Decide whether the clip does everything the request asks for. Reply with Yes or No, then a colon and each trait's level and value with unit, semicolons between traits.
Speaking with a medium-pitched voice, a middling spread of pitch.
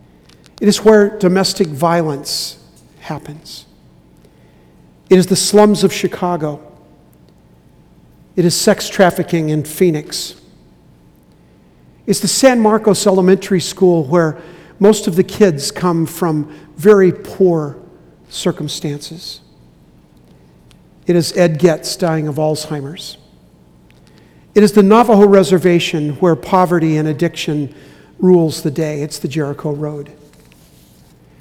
Yes: medium, 165 Hz; average, 4.1 semitones